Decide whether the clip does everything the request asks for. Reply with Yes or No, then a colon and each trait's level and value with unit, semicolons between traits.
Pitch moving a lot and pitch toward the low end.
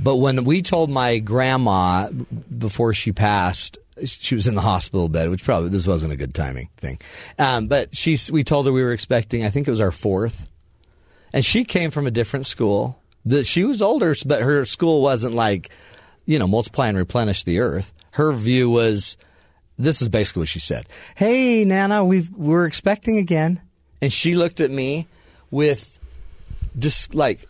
Yes: wide, 7.7 semitones; low, 120 Hz